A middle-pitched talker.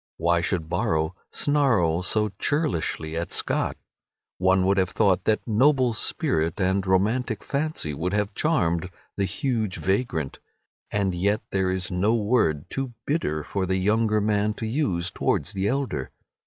No: low, 100 Hz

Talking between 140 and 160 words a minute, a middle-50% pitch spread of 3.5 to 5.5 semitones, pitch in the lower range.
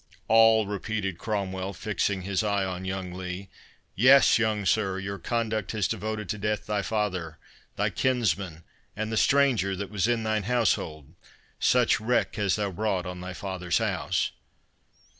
No: average, 150 wpm; average, 2.7 semitones; low, 100 Hz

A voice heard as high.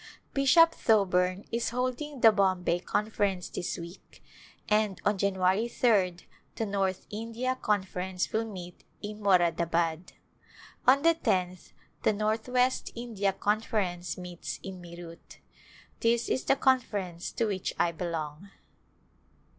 Yes: high, 200 Hz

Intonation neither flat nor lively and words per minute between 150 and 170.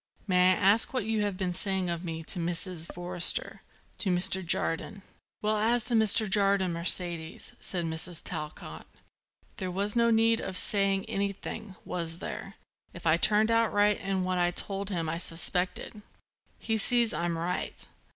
Yes: average, 3.2 semitones; average, 165 wpm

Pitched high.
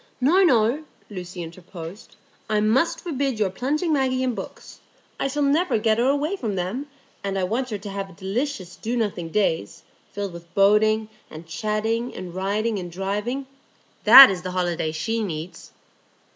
Yes: high, 215 Hz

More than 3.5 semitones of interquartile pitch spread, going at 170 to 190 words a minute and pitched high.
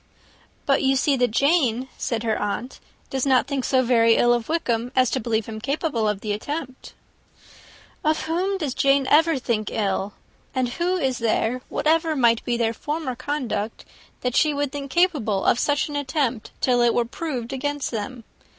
Yes: average, 3.9 semitones; average, 180 wpm; very high, 255 Hz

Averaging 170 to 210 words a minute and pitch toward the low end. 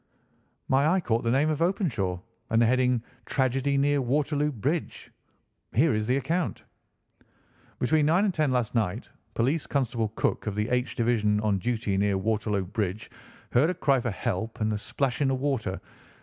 Yes: average, 175 wpm; low, 125 Hz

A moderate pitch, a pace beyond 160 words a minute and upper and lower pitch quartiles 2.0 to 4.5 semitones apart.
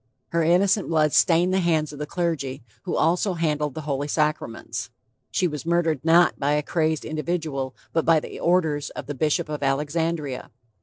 Yes: medium, 155 Hz; average, 175 wpm; narrow, 2.5 semitones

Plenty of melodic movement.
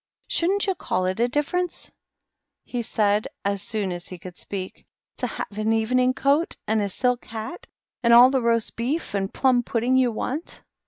No: average, 4.0 semitones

